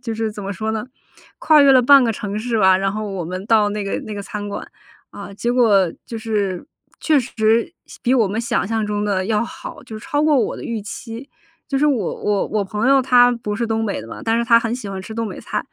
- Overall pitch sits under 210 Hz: No, high, 220 Hz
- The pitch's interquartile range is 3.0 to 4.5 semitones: No, narrow, 2.6 semitones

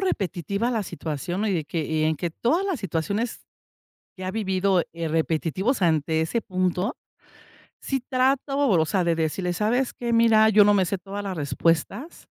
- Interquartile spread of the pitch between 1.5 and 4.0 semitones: No, wide, 5.4 semitones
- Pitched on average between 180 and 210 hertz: Yes, high, 190 Hz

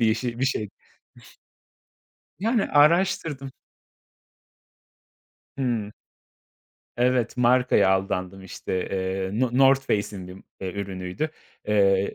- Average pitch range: No, wide, 5.7 semitones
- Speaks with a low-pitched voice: Yes, low, 110 Hz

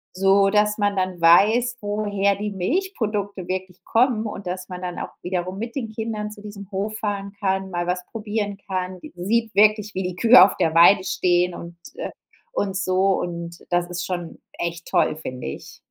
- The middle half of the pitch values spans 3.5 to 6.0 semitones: No, average, 2.7 semitones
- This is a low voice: No, high, 195 Hz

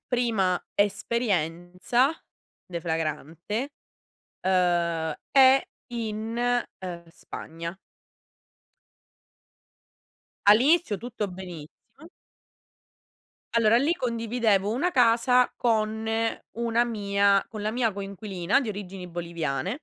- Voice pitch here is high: Yes, high, 210 Hz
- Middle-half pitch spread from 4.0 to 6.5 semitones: Yes, average, 4.9 semitones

